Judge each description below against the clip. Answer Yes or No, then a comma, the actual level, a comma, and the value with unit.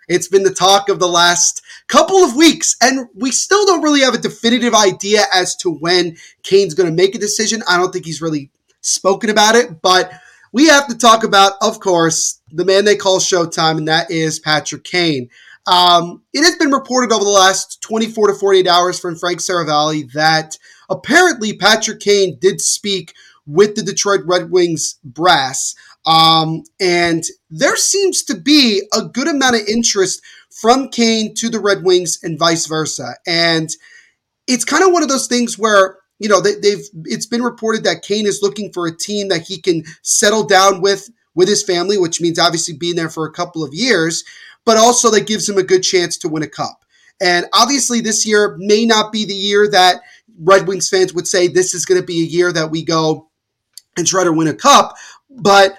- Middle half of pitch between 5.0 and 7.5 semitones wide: No, average, 4.0 semitones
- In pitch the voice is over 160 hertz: Yes, high, 190 Hz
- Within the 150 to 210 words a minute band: Yes, average, 200 wpm